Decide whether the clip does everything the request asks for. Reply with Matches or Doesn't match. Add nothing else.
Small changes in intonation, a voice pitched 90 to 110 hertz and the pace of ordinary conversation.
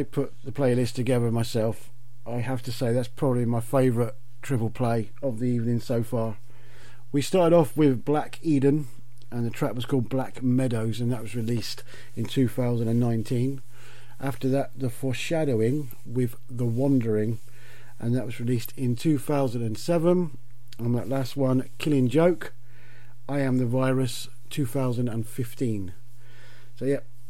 Doesn't match